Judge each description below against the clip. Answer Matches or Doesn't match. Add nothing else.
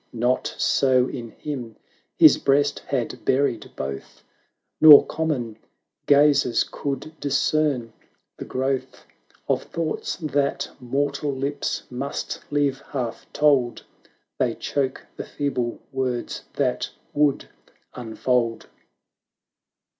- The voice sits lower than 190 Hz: Matches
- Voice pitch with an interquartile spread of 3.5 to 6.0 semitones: Doesn't match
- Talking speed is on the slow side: Matches